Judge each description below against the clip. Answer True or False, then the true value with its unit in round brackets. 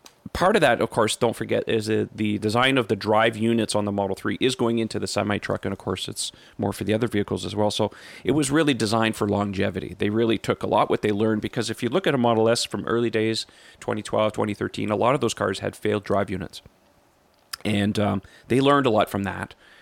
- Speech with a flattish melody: True (2.2 semitones)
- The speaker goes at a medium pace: False (245 wpm)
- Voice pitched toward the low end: True (110 Hz)